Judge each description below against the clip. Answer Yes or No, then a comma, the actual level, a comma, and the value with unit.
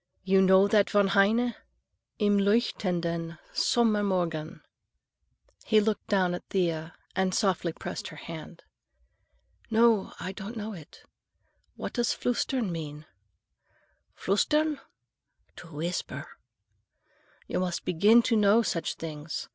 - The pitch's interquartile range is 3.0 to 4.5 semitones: Yes, average, 4.2 semitones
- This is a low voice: No, high, 190 Hz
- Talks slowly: Yes, slow, 115 wpm